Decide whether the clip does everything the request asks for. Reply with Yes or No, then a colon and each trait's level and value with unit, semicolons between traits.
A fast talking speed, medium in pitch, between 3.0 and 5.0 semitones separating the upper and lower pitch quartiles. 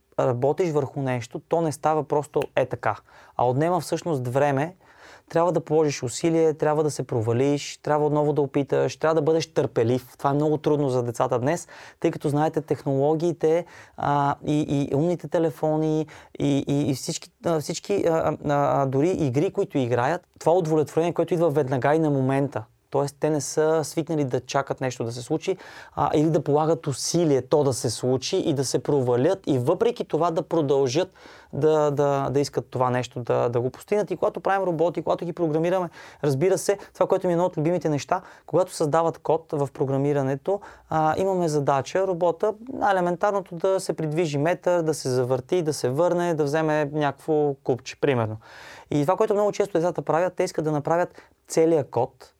Yes: fast, 185 wpm; medium, 155 Hz; average, 3.5 semitones